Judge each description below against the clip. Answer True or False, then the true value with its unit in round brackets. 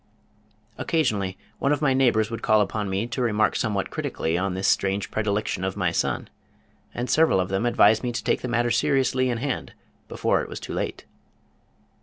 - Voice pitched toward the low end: True (110 Hz)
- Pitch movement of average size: True (4.2 semitones)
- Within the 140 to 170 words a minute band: False (190 wpm)